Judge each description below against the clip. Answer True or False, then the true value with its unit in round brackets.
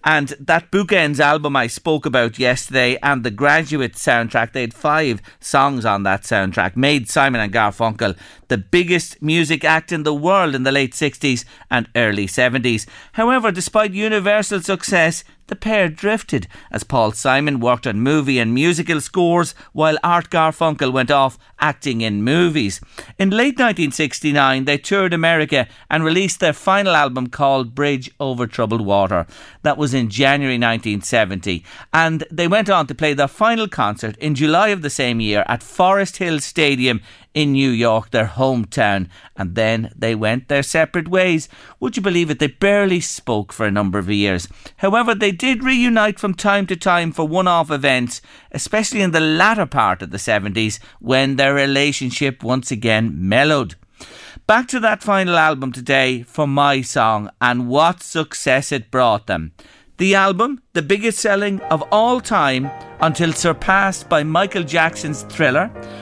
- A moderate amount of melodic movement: False (6.4 semitones)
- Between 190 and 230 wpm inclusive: False (165 wpm)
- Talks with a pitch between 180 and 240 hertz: False (145 Hz)